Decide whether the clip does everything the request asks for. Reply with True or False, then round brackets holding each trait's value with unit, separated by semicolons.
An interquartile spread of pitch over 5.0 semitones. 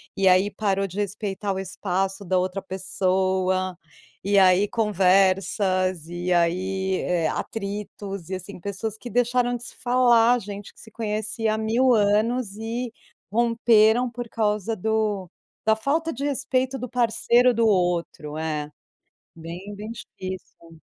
False (3.4 semitones)